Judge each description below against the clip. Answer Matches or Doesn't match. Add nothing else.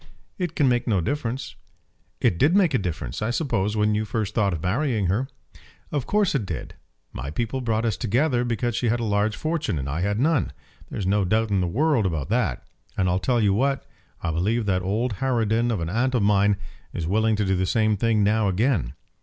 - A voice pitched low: Matches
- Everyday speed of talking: Doesn't match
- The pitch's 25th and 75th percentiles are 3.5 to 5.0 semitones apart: Matches